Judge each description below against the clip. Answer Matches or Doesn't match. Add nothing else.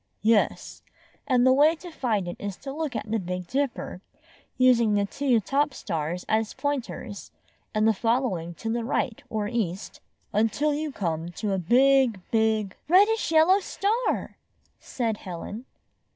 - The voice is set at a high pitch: Matches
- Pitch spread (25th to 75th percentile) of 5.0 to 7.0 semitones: Matches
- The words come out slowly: Doesn't match